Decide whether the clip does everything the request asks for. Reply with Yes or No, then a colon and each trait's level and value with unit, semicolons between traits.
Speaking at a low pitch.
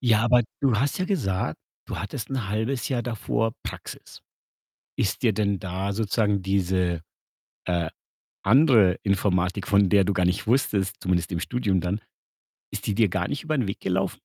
Yes: low, 100 Hz